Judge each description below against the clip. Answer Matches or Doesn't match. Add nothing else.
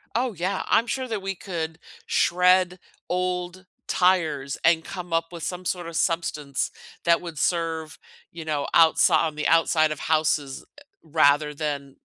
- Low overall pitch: Doesn't match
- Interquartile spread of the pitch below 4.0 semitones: Matches